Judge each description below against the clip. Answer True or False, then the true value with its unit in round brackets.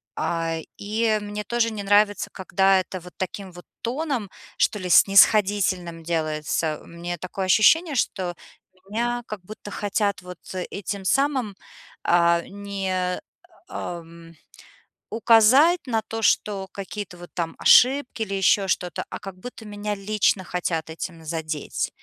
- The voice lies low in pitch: False (195 Hz)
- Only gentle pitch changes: False (3.4 semitones)